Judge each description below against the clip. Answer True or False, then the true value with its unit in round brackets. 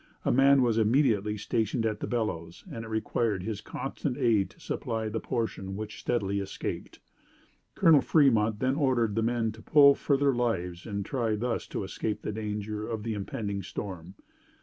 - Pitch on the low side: True (110 Hz)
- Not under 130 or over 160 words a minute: False (175 wpm)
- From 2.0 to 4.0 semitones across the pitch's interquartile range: True (2.9 semitones)